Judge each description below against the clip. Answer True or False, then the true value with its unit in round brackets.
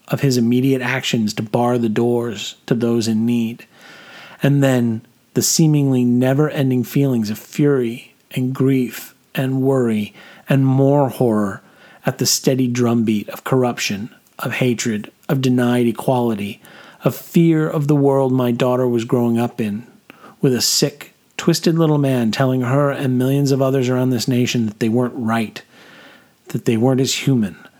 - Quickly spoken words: False (160 wpm)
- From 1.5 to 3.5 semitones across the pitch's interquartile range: True (2.4 semitones)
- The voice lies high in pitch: False (125 Hz)